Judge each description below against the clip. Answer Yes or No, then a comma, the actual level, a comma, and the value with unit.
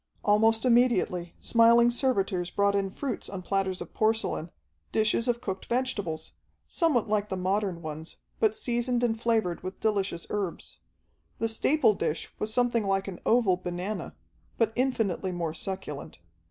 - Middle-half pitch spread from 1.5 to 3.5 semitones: No, average, 4.1 semitones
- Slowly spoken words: No, average, 145 wpm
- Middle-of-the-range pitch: No, high, 210 Hz